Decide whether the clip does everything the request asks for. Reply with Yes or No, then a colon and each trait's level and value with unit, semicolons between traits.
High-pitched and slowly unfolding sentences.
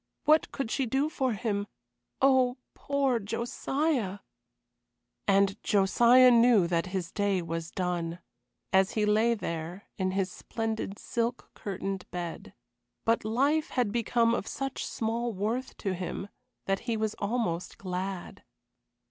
Yes: high, 215 Hz; slow, 130 wpm